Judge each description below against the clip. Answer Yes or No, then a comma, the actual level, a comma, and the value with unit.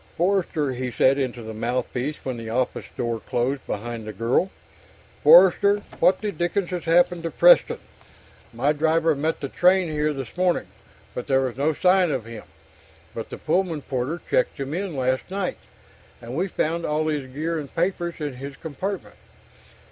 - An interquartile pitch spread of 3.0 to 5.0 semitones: No, wide, 5.5 semitones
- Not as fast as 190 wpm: Yes, average, 170 wpm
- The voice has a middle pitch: Yes, medium, 150 Hz